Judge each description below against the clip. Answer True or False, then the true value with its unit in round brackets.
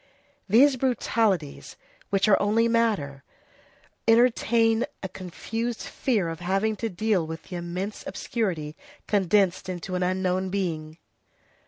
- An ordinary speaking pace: False (120 wpm)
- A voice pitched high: True (195 Hz)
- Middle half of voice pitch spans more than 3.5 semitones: True (4.2 semitones)